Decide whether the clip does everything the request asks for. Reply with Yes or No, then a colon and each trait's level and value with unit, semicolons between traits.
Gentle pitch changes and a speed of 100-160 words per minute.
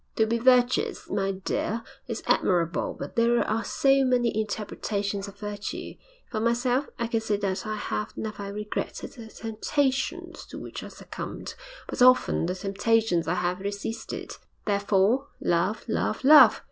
No: average, 3.0 semitones; average, 150 wpm